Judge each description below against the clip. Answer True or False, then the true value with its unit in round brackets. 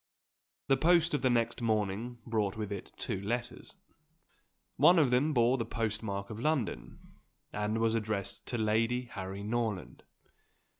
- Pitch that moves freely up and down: False (2.8 semitones)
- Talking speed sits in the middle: True (145 wpm)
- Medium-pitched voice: False (115 Hz)